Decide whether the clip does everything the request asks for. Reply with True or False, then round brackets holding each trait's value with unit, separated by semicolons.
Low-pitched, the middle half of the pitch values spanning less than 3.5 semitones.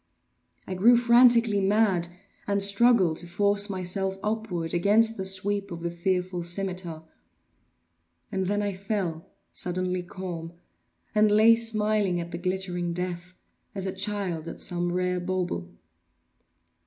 False (190 Hz; 2.7 semitones)